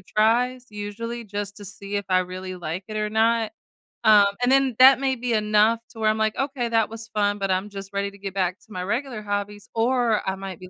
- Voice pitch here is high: Yes, high, 210 Hz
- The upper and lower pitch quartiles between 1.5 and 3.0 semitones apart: Yes, narrow, 2.6 semitones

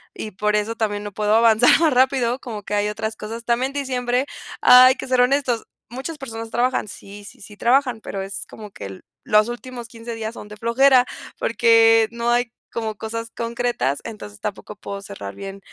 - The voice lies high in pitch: Yes, high, 230 Hz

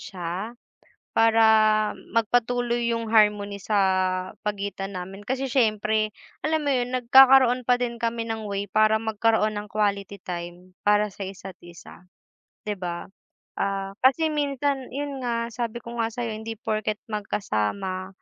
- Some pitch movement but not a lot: Yes, average, 3.3 semitones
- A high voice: Yes, high, 215 Hz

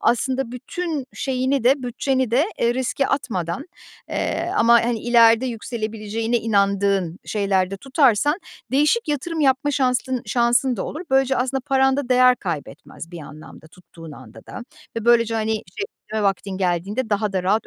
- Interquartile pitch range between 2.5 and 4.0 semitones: No, average, 4.8 semitones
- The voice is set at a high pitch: Yes, high, 235 Hz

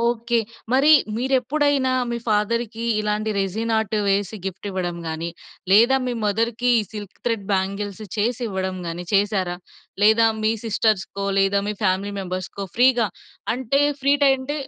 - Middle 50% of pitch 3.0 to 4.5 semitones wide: Yes, average, 3.4 semitones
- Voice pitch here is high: Yes, high, 215 Hz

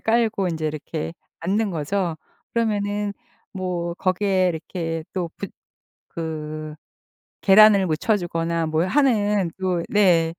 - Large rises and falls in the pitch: No, average, 3.8 semitones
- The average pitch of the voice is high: No, medium, 180 Hz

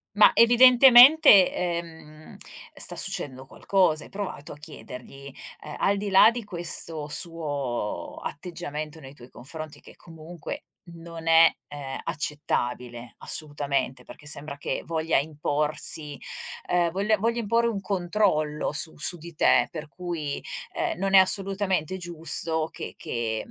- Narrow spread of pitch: No, average, 4.3 semitones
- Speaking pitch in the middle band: Yes, medium, 160 Hz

